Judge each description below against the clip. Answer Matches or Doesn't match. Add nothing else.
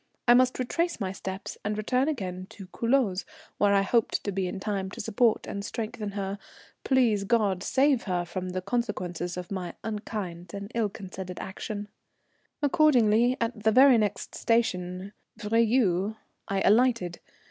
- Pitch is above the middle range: Matches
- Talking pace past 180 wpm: Doesn't match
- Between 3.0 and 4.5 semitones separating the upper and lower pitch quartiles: Matches